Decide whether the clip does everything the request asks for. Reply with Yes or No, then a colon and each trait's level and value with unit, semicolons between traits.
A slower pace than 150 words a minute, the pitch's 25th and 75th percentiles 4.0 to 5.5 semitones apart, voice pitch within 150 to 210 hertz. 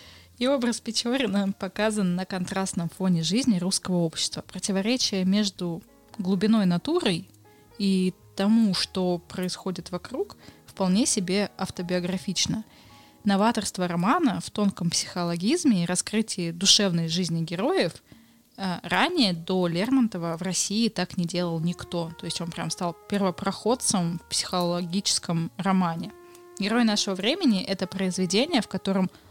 No: average, 115 wpm; average, 3.3 semitones; high, 190 Hz